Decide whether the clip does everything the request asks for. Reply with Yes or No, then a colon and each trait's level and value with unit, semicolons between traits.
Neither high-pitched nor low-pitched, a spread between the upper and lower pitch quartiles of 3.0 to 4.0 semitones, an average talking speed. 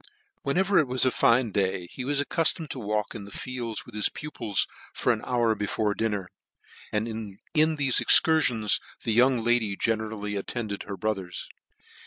No: low, 115 Hz; average, 3.7 semitones; average, 165 wpm